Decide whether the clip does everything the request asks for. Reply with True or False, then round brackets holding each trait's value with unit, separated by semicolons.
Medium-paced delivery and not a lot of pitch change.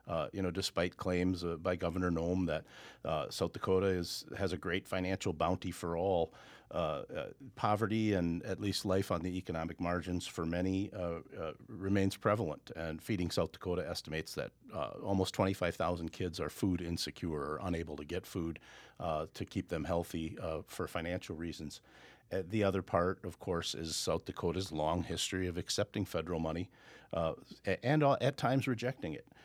True (180 wpm; 2.2 semitones)